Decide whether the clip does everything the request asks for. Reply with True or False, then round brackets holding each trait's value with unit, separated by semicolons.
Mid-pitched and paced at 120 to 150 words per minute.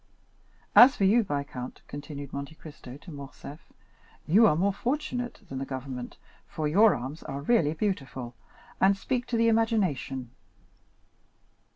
True (155 Hz; 140 wpm)